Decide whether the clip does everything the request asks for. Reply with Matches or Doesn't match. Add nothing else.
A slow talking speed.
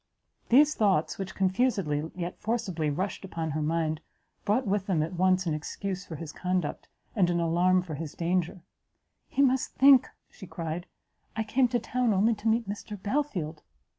Doesn't match